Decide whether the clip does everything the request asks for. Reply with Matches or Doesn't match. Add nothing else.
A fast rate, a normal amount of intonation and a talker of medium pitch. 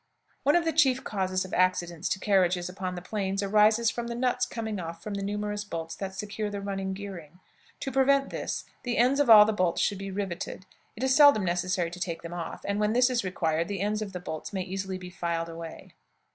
Doesn't match